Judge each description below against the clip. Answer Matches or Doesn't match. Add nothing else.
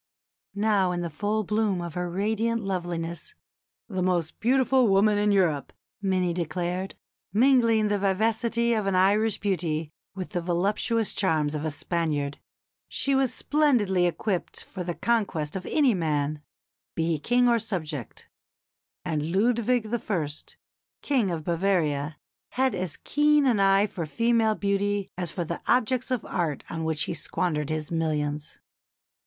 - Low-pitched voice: Doesn't match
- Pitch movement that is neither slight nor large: Matches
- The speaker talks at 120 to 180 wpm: Matches